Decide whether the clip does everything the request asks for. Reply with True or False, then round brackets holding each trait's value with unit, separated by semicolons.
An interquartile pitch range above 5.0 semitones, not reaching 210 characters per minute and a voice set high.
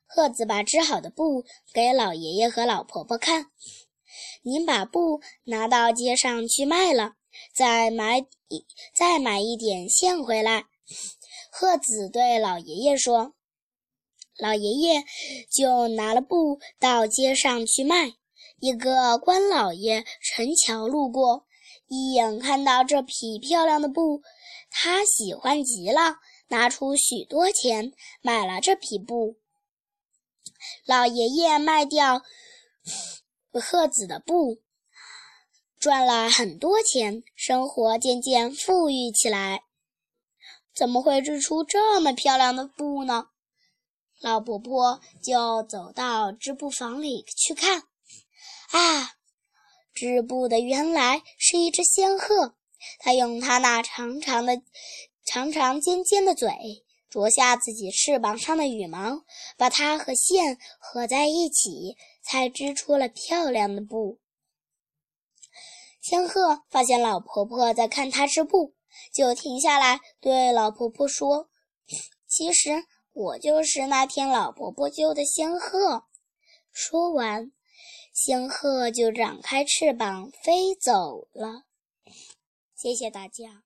True (5.5 semitones; 170 characters per minute; 265 Hz)